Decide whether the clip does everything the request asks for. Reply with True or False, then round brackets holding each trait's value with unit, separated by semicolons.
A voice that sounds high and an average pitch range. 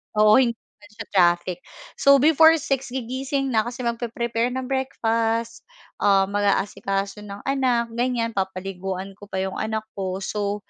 True (225 Hz; 4.1 semitones)